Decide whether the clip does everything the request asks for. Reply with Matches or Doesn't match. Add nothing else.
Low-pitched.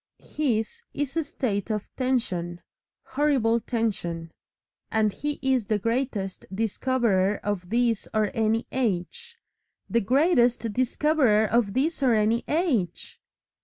Doesn't match